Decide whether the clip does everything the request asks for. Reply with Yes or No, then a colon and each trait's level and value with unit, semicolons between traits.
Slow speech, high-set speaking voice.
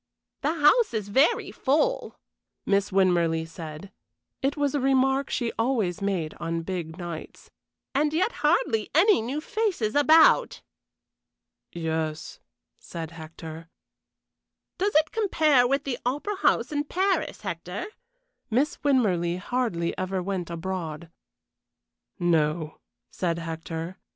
Yes: slow, 115 wpm; high, 200 Hz